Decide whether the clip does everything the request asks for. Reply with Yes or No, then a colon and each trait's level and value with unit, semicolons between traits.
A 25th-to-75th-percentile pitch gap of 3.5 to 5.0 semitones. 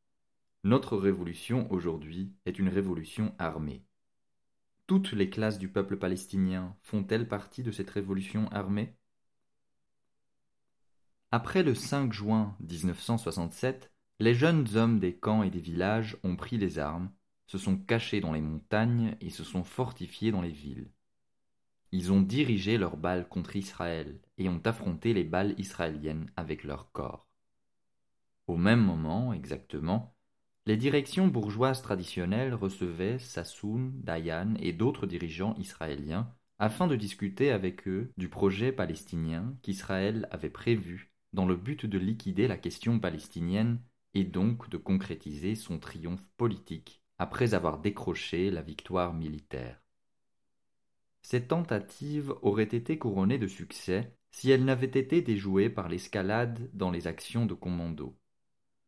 Yes: average, 4.3 semitones